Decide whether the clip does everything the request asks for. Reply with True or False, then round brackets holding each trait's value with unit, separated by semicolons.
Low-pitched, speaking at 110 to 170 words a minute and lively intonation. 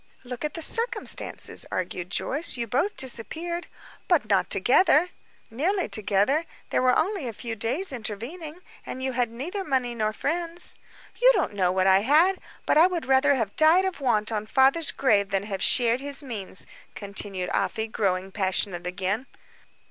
False (250 Hz; 165 wpm; 7.3 semitones)